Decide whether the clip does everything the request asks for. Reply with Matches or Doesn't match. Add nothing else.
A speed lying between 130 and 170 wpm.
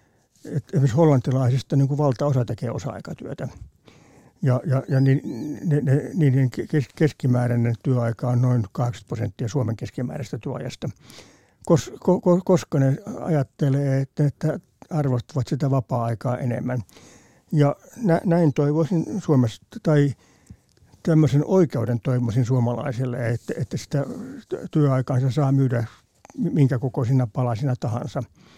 Doesn't match